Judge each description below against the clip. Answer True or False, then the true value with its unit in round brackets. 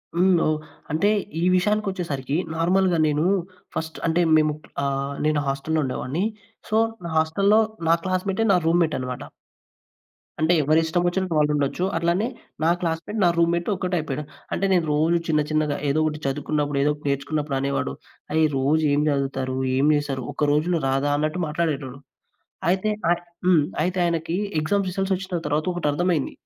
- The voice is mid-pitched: True (160 Hz)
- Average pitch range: True (3.4 semitones)